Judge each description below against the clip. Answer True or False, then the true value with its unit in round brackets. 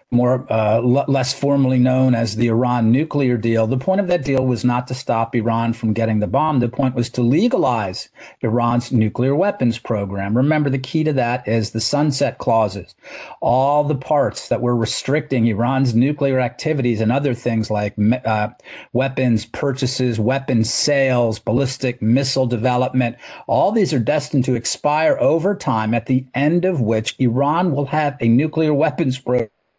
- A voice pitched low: True (125 Hz)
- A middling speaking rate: True (170 wpm)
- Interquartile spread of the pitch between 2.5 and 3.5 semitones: True (3.2 semitones)